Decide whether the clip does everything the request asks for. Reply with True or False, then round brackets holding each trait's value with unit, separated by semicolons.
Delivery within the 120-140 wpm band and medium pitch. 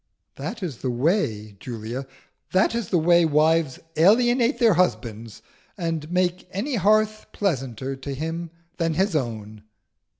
True (135 wpm; 165 Hz)